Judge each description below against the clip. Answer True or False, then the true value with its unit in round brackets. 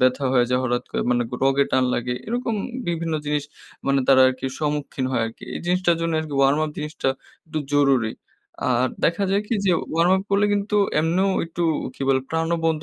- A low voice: False (150 Hz)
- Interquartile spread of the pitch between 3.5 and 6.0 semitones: True (4.4 semitones)